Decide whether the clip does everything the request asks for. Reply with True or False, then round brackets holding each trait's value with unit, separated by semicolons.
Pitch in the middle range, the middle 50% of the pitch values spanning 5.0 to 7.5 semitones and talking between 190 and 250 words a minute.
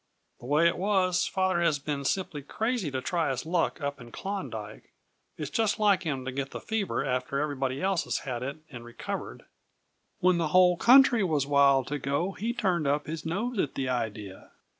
True (150 Hz; 5.6 semitones; 195 wpm)